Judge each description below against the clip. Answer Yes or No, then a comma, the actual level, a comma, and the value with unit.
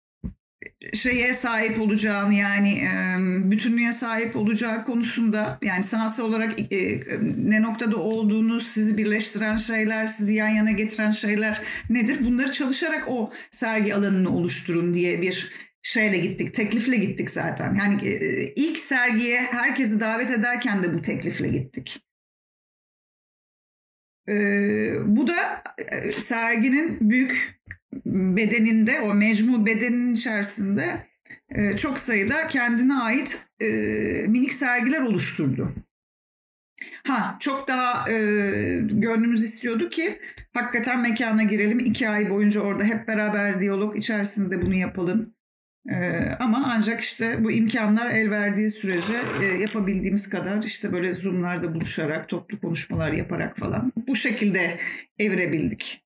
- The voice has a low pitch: No, high, 220 Hz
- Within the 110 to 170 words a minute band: Yes, average, 115 wpm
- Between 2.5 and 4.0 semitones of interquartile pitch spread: Yes, average, 2.8 semitones